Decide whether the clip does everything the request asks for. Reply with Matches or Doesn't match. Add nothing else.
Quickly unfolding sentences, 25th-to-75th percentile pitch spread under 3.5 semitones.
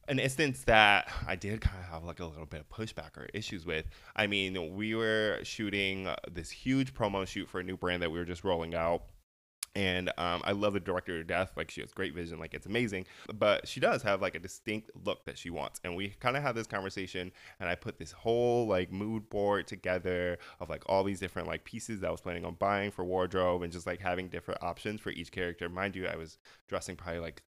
Matches